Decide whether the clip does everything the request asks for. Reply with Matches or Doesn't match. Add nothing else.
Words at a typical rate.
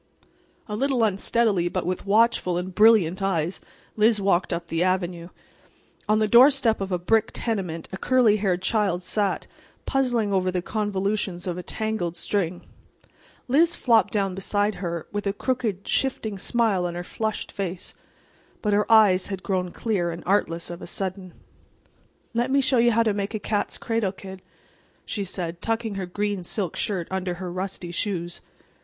Matches